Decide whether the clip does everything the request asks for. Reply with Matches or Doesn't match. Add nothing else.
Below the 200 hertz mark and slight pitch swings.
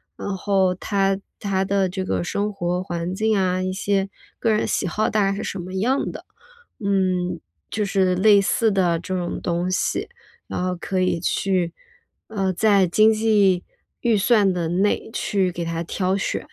Matches